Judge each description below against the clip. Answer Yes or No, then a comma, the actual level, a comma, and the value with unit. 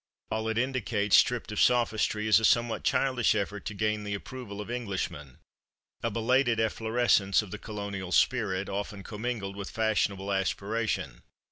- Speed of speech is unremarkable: Yes, average, 150 wpm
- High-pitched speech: No, low, 105 Hz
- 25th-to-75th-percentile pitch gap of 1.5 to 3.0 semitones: Yes, narrow, 2.5 semitones